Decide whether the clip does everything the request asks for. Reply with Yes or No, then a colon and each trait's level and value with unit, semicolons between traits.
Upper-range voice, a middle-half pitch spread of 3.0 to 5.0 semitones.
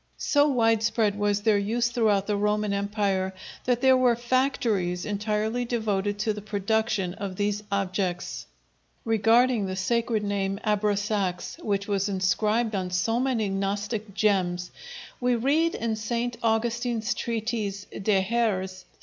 No: high, 210 Hz; narrow, 2.6 semitones